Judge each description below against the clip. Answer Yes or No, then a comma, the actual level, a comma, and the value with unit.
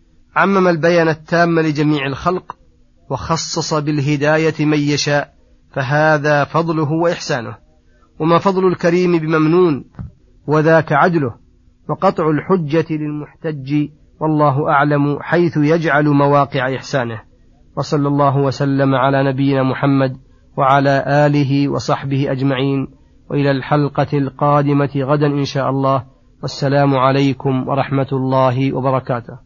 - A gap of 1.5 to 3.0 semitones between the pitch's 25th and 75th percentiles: Yes, narrow, 2.4 semitones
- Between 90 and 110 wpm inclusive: Yes, average, 100 wpm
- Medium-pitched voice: Yes, medium, 145 Hz